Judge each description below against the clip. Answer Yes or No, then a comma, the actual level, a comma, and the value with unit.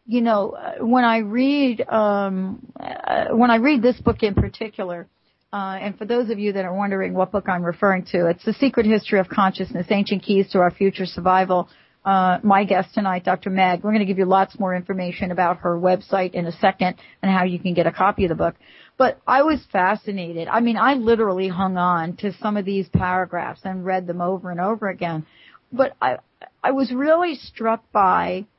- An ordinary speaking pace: No, fast, 210 wpm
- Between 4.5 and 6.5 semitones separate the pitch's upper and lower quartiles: No, average, 3.5 semitones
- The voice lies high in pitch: Yes, high, 195 Hz